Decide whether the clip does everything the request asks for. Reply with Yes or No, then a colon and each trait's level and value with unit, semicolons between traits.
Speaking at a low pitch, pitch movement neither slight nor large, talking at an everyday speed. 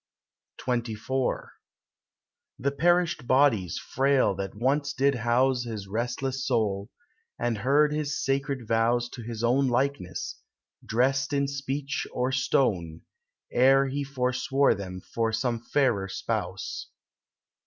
No: low, 130 Hz; average, 3.3 semitones; slow, 115 wpm